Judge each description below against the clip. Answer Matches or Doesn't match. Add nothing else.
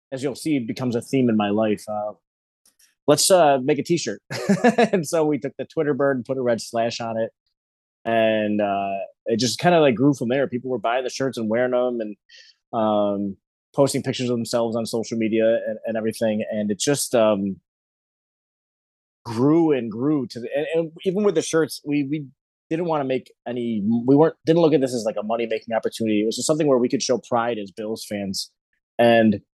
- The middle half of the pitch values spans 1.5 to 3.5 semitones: Doesn't match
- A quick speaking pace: Matches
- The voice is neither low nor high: Doesn't match